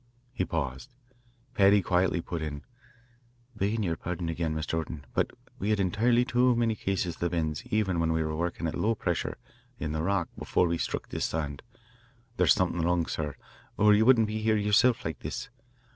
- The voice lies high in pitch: No, very low, 90 Hz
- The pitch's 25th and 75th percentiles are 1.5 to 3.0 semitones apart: No, average, 4.7 semitones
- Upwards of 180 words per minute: Yes, average, 190 wpm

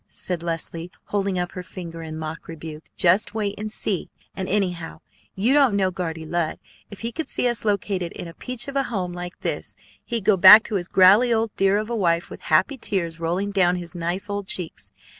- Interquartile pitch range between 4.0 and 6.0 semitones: No, average, 3.6 semitones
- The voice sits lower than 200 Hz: Yes, medium, 185 Hz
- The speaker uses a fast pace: Yes, fast, 215 wpm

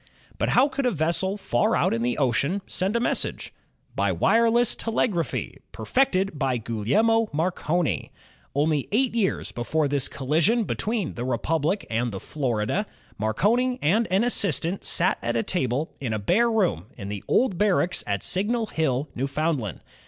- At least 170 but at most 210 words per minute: No, average, 155 wpm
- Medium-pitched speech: Yes, medium, 165 Hz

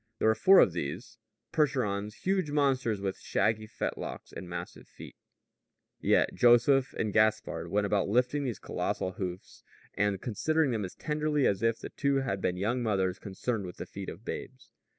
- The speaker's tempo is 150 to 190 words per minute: Yes, average, 170 wpm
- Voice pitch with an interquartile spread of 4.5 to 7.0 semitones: Yes, average, 5.2 semitones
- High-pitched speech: No, low, 110 Hz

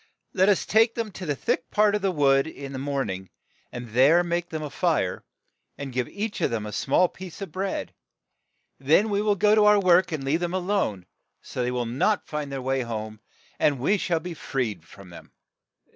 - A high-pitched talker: No, medium, 155 Hz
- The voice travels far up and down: Yes, wide, 6.8 semitones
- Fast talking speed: Yes, fast, 220 wpm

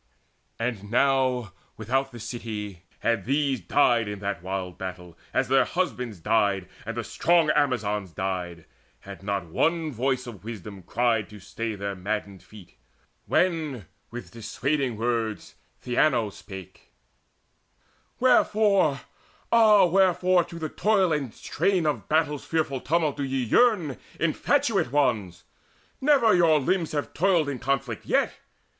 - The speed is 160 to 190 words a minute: No, slow, 135 wpm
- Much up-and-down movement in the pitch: Yes, wide, 7.0 semitones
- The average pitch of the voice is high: No, low, 125 Hz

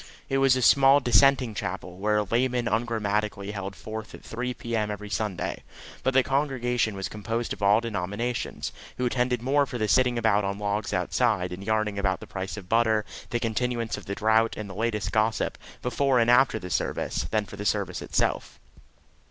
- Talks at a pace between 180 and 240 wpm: Yes, average, 190 wpm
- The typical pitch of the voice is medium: No, low, 110 Hz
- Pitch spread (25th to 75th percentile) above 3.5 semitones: No, average, 3.1 semitones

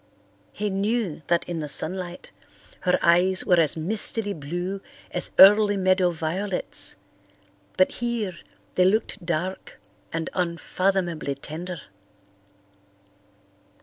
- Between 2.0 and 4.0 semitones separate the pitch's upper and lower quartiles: Yes, narrow, 2.6 semitones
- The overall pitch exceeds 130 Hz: Yes, medium, 185 Hz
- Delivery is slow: Yes, slow, 105 wpm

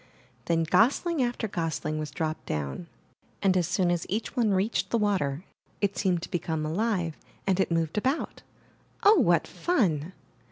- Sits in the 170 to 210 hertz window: Yes, medium, 185 Hz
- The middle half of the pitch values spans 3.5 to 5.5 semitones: Yes, average, 5.0 semitones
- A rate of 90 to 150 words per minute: No, average, 160 wpm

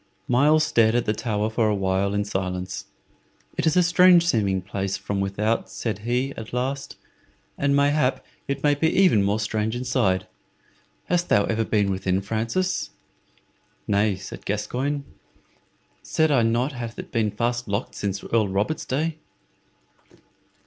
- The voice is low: Yes, low, 115 Hz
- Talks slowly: No, average, 150 wpm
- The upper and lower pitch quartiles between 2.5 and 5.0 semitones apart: No, wide, 5.4 semitones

